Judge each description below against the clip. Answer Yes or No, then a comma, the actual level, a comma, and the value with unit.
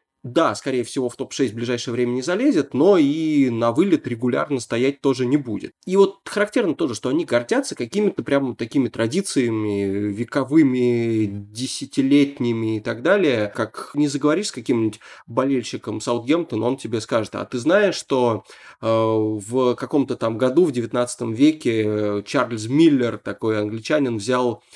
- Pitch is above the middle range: No, low, 125 Hz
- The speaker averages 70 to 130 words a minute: No, average, 150 wpm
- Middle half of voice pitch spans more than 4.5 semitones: No, average, 4.0 semitones